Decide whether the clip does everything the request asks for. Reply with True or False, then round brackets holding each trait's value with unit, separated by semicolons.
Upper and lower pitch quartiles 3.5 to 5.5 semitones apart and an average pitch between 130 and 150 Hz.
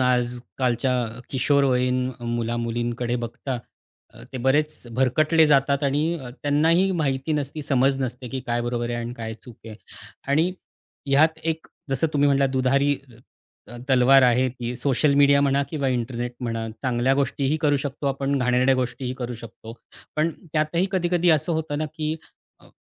False (3.0 semitones; 135 Hz)